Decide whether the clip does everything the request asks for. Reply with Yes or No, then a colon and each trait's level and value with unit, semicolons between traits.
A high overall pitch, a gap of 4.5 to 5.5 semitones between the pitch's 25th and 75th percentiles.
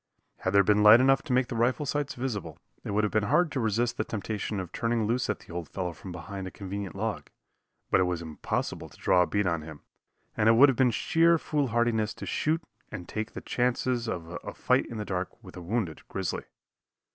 No: low, 110 Hz; average, 4.8 semitones